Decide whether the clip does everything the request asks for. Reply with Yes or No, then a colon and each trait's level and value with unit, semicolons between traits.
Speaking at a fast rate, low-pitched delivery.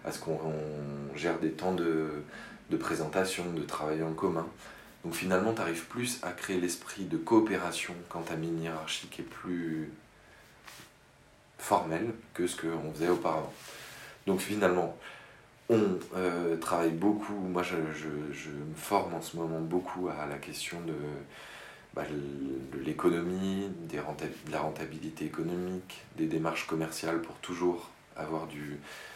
No: slow, 145 wpm; very low, 80 Hz